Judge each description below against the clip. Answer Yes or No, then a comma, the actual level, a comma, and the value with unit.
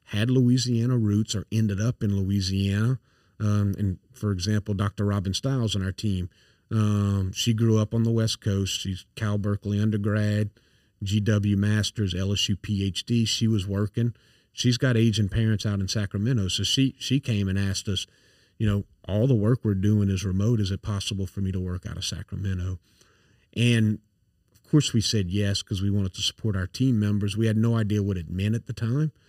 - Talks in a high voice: No, low, 105 Hz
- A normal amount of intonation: No, narrow, 2.3 semitones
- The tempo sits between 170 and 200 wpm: Yes, average, 195 wpm